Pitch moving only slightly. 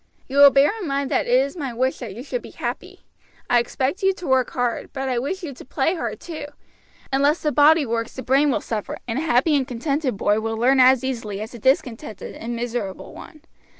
No: average, 3.3 semitones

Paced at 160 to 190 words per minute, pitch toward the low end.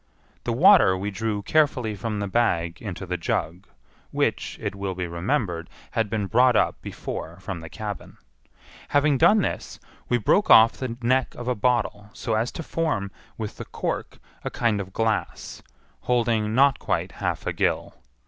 Yes: average, 170 wpm; low, 110 Hz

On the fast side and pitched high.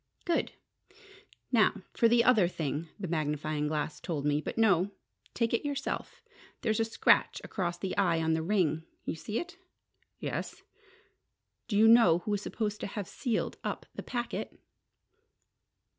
No: average, 155 wpm; high, 195 Hz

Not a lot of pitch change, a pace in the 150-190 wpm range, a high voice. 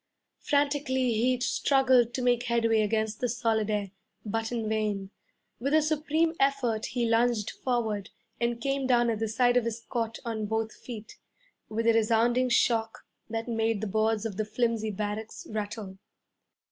Yes: narrow, 2.1 semitones; average, 160 wpm; high, 230 Hz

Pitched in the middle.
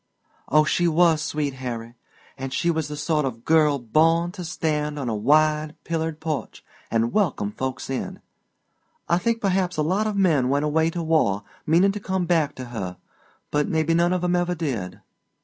Yes: medium, 155 Hz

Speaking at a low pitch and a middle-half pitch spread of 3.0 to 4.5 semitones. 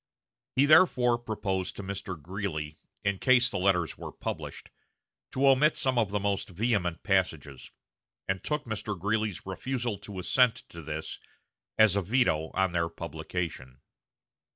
No: low, 100 Hz; average, 5.3 semitones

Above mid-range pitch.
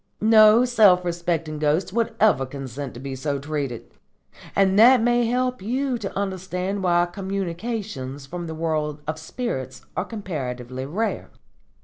No: medium, 175 Hz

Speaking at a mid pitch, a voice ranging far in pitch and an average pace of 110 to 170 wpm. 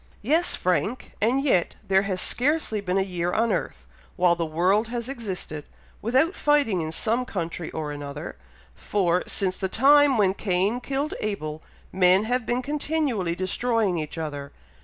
No: high, 200 Hz; wide, 6.0 semitones; average, 160 wpm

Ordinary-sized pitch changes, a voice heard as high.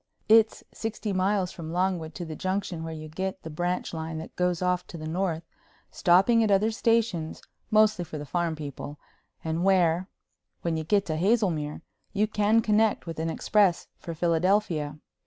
No: average, 4.0 semitones; medium, 180 Hz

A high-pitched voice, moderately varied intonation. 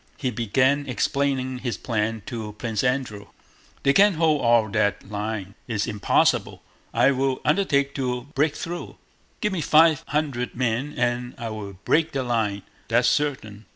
No: low, 125 Hz; average, 4.1 semitones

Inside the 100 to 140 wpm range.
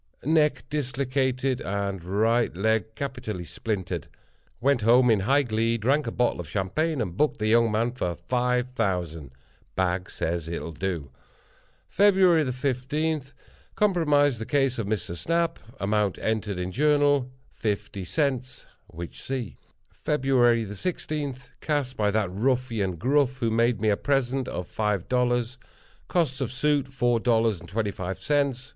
Yes: slow, 135 wpm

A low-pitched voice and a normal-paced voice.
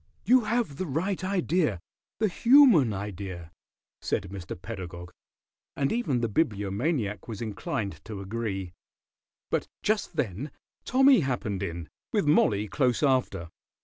No: low, 115 Hz; slow, 125 wpm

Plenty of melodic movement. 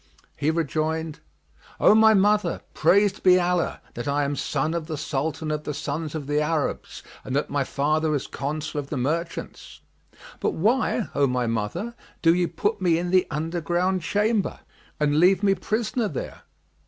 No: average, 4.0 semitones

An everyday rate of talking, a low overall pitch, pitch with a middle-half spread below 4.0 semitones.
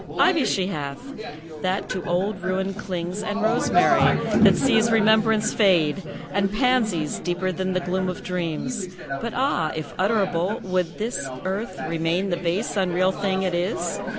No: average, 150 wpm; high, 190 Hz; average, 3.3 semitones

